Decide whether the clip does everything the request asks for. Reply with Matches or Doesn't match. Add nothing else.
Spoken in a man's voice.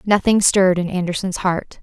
Doesn't match